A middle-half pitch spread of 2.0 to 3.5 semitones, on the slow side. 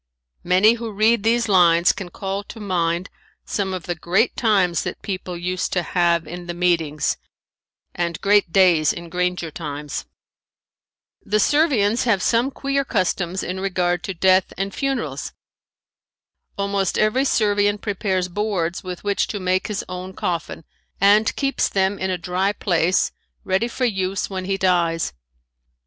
No: average, 2.7 semitones; average, 150 wpm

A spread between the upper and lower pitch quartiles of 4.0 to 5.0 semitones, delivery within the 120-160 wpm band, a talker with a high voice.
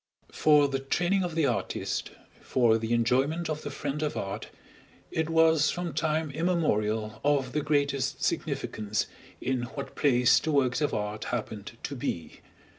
No: average, 4.6 semitones; average, 155 wpm; medium, 140 Hz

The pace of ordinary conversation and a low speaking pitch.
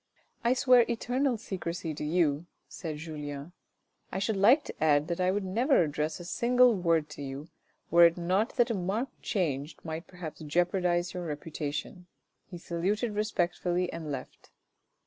No: average, 165 wpm; medium, 175 Hz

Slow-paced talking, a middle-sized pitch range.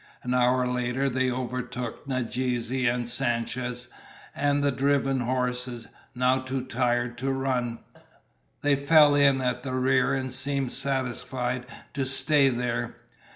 No: slow, 130 wpm; narrow, 1.5 semitones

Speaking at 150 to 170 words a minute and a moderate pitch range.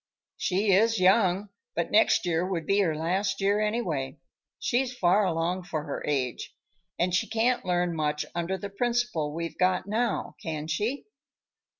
Yes: average, 160 wpm; average, 4.3 semitones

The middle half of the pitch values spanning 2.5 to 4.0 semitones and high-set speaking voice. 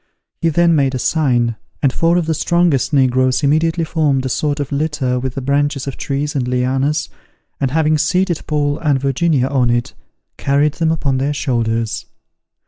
No: average, 3.2 semitones; medium, 140 Hz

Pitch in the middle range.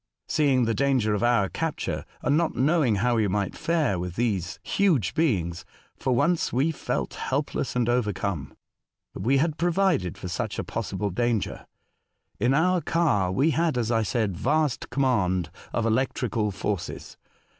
No: low, 120 Hz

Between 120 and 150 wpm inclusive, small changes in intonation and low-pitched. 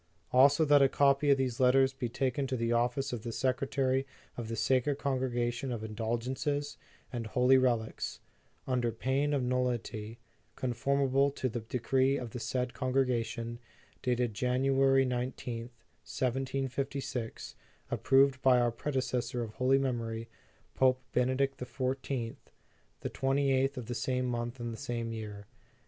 Yes: average, 145 wpm; narrow, 2.2 semitones; low, 125 Hz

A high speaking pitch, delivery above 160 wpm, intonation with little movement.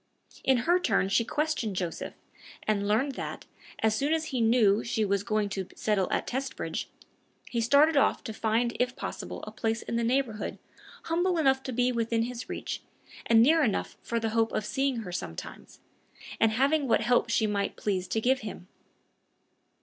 No: high, 230 Hz; average, 180 wpm; average, 3.8 semitones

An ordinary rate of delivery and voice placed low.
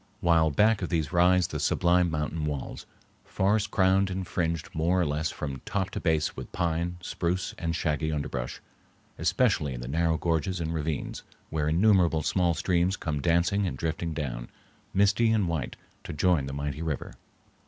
Yes: average, 170 wpm; very low, 85 Hz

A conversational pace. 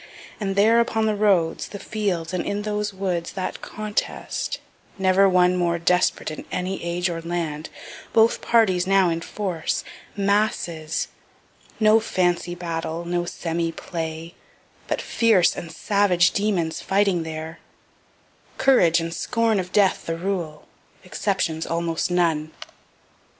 No: slow, 130 wpm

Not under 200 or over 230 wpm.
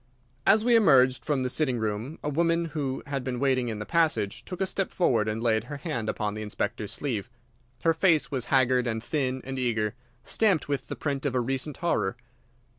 Yes: fast, 205 wpm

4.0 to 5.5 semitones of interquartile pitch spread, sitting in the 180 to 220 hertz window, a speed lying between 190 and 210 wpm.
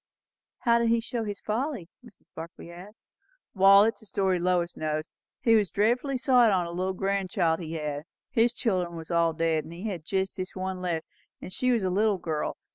Yes: average, 4.5 semitones; high, 190 Hz; average, 200 wpm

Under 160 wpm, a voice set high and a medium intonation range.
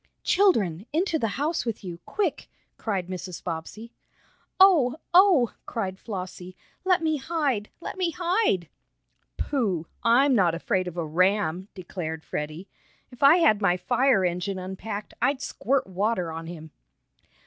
No: average, 140 wpm; high, 205 Hz; wide, 7.6 semitones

